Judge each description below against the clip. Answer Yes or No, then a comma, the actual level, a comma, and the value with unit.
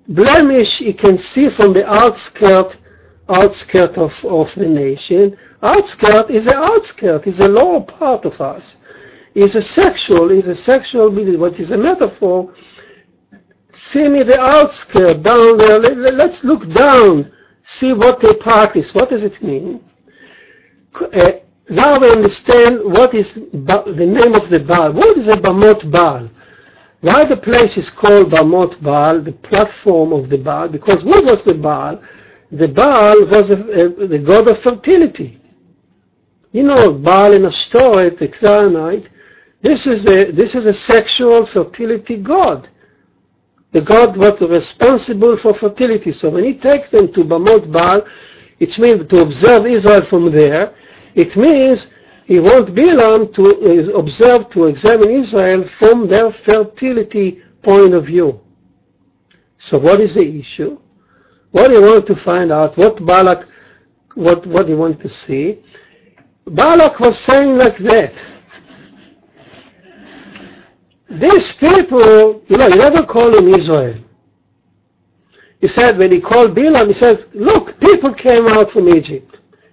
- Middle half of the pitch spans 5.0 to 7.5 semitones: Yes, average, 5.3 semitones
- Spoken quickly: No, average, 145 wpm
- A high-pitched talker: Yes, high, 210 Hz